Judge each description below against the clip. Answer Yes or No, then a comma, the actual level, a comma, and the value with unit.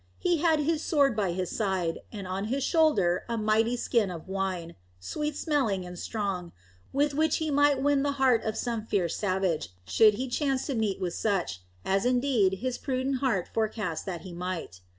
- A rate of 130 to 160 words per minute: No, average, 190 wpm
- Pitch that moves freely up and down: Yes, wide, 6.6 semitones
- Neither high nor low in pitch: No, high, 220 Hz